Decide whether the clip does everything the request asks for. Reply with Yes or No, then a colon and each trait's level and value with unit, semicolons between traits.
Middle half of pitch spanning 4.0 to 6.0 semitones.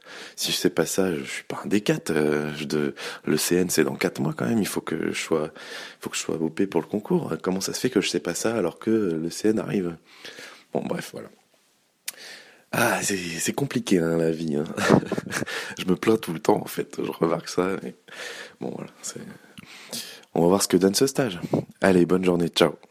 No: average, 3.4 semitones